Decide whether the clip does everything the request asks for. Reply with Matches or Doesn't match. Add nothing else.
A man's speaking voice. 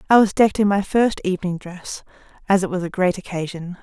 Doesn't match